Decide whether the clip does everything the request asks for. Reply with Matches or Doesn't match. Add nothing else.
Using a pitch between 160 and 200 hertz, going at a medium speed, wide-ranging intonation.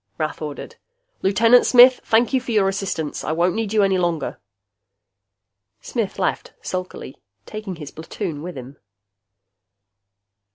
Doesn't match